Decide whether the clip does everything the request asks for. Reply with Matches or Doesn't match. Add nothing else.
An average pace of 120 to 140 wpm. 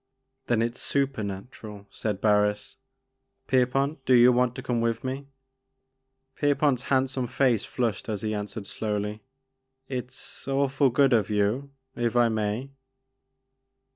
Doesn't match